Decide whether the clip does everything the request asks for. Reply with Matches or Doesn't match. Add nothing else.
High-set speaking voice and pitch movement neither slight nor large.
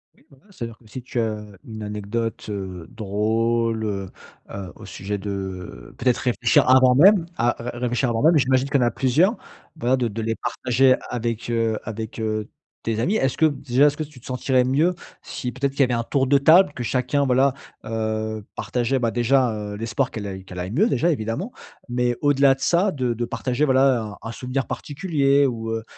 Doesn't match